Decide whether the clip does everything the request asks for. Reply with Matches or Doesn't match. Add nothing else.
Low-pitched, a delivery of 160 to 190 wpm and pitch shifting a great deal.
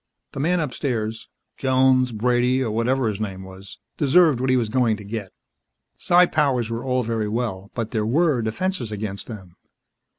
Doesn't match